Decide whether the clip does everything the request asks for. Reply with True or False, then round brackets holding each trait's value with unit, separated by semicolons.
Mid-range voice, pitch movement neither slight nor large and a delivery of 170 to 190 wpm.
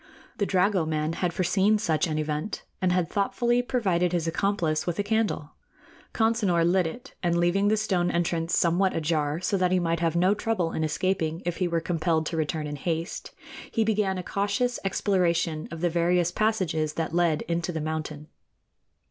True (175 Hz; 3.3 semitones; 180 wpm)